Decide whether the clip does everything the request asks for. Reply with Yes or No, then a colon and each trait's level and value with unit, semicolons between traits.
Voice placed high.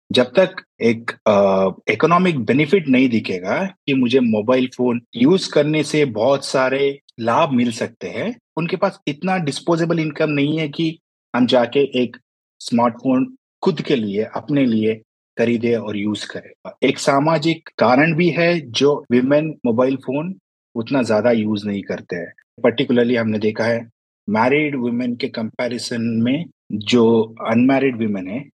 No: low, 130 Hz